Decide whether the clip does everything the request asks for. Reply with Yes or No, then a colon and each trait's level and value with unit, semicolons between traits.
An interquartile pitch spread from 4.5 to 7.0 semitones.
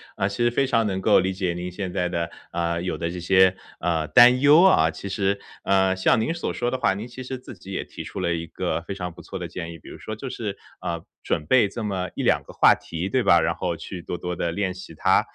No: average, 3.9 semitones